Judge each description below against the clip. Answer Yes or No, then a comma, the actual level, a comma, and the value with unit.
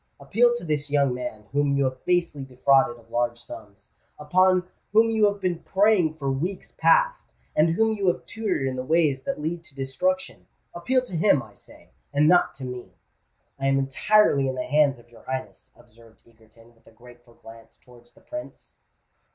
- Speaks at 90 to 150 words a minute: No, average, 175 wpm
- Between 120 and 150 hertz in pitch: Yes, medium, 140 Hz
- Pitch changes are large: Yes, wide, 6.7 semitones